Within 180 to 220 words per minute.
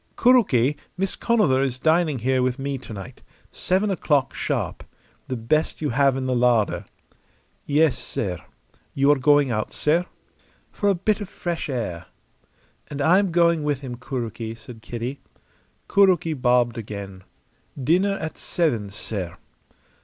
No: average, 145 wpm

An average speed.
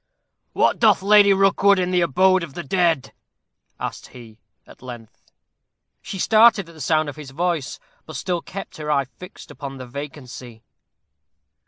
Yes: average, 160 wpm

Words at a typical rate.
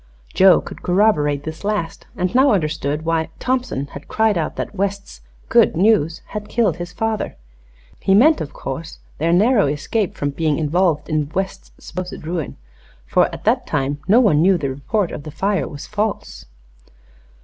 Yes: average, 170 wpm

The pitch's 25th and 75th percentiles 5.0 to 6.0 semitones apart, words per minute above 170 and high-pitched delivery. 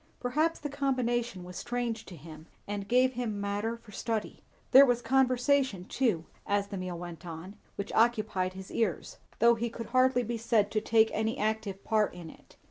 No: average, 3.8 semitones; average, 185 wpm; high, 220 Hz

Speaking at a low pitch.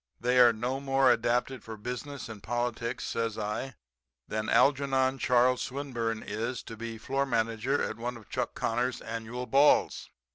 Yes: low, 120 Hz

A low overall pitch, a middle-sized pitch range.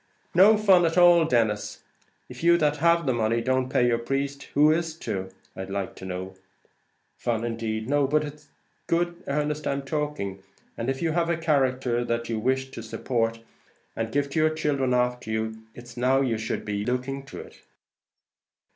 Yes: low, 130 Hz; average, 4.7 semitones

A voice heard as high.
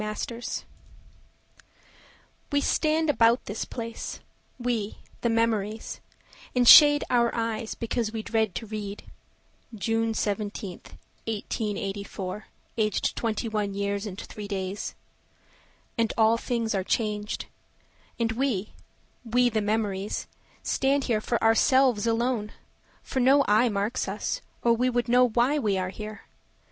Yes: high, 225 Hz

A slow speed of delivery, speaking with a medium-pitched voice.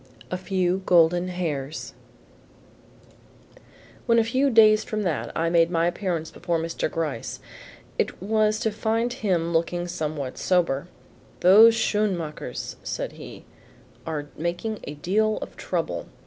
Yes: slow, 130 wpm; medium, 180 Hz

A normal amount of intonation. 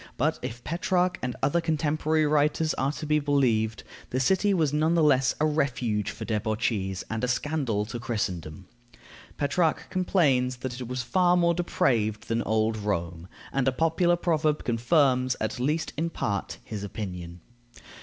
No: wide, 6.2 semitones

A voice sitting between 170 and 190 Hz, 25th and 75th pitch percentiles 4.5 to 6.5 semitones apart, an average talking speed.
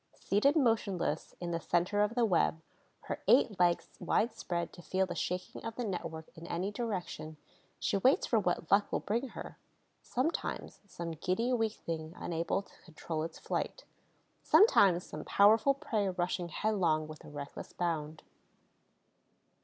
Yes: medium, 185 Hz; average, 4.8 semitones; average, 155 wpm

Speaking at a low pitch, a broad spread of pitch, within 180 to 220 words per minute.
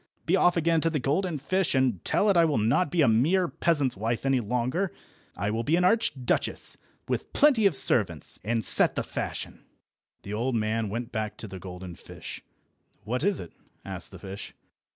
Yes: low, 130 Hz; wide, 7.5 semitones; average, 190 wpm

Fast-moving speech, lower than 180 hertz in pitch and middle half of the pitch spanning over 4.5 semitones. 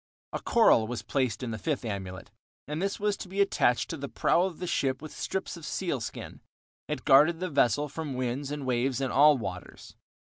Yes: fast, 210 wpm; medium, 140 Hz; average, 5.2 semitones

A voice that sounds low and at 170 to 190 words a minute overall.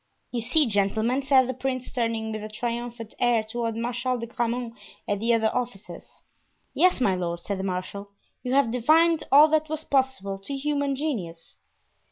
No: high, 240 Hz; average, 175 wpm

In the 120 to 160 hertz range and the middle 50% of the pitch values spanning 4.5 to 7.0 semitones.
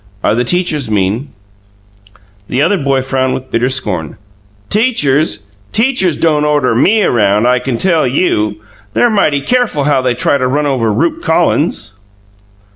Yes: low, 135 Hz; average, 5.2 semitones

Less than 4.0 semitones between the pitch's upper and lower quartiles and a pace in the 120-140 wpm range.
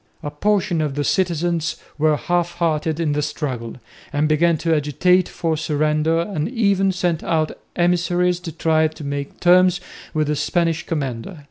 No: narrow, 2.6 semitones; average, 160 wpm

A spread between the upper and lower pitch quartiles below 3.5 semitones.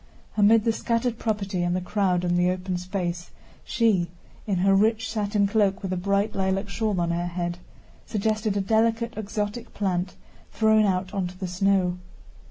Yes: average, 3.1 semitones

